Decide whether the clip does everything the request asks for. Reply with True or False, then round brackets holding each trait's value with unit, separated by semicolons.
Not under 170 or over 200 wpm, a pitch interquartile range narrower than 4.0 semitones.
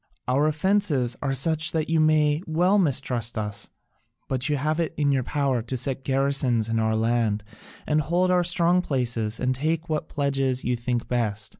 False (180 wpm; 4.4 semitones)